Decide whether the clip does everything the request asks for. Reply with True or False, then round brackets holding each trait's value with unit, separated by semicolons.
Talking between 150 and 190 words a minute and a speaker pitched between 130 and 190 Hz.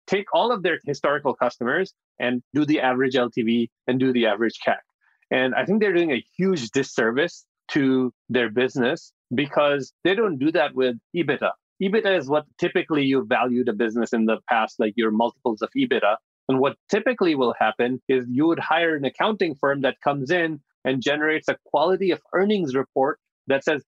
True (185 wpm; 135 Hz)